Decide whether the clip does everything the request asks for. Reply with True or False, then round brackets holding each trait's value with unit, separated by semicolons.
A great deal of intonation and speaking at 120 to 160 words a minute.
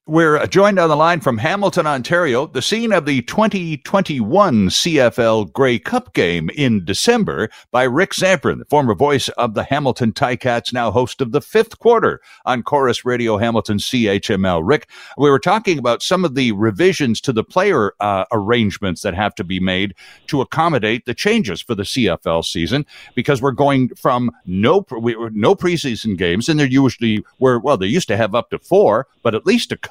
False (6.9 semitones; 190 wpm)